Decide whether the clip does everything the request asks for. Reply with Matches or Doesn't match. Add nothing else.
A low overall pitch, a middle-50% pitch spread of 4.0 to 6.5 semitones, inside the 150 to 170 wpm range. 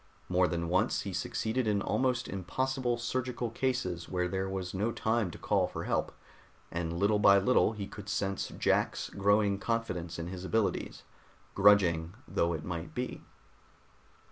Matches